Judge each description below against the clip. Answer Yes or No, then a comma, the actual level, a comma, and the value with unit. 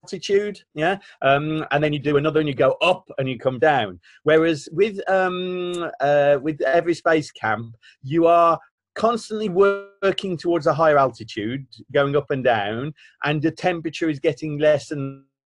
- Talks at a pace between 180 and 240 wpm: No, average, 165 wpm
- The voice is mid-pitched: Yes, medium, 155 Hz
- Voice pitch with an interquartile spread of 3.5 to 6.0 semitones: Yes, average, 4.1 semitones